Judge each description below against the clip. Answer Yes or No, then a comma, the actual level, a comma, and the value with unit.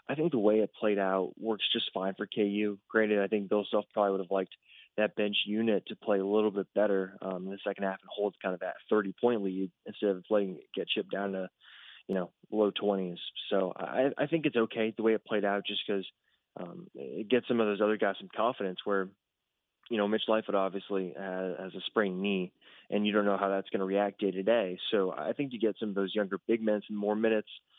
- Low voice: Yes, low, 100 Hz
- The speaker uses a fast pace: Yes, fast, 240 wpm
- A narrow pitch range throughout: Yes, narrow, 1.8 semitones